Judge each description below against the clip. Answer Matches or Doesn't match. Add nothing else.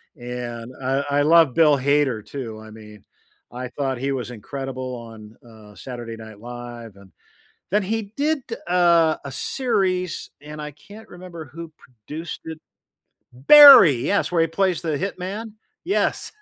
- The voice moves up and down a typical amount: Doesn't match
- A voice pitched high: Doesn't match